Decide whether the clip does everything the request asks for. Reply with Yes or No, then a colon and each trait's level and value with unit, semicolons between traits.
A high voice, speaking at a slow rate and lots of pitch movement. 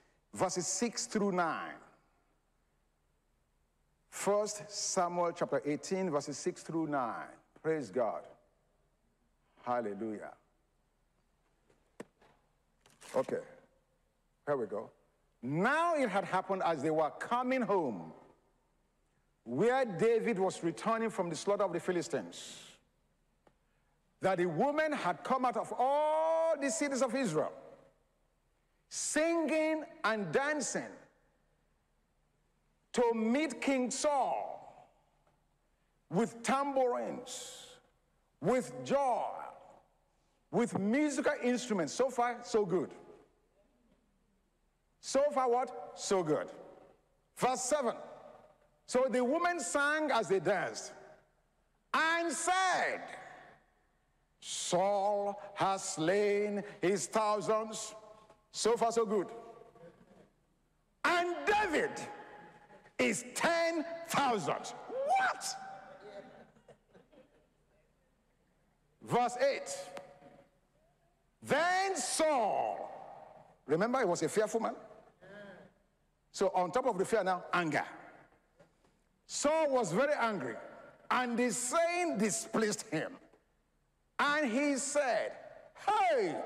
Yes: high, 225 Hz; slow, 90 wpm; wide, 6.6 semitones